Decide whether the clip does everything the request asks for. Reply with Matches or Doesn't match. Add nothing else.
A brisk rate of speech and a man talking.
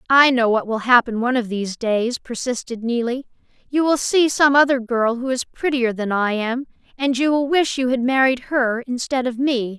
Doesn't match